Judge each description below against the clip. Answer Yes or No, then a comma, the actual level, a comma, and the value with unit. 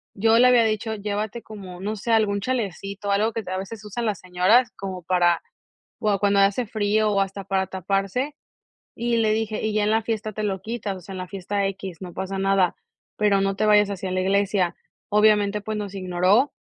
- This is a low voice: No, high, 205 Hz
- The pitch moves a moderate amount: No, narrow, 2.0 semitones